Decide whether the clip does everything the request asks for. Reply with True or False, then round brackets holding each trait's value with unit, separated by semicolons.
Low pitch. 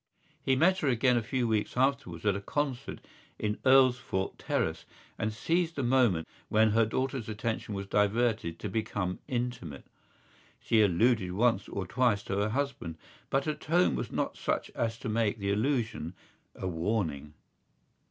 True (110 Hz)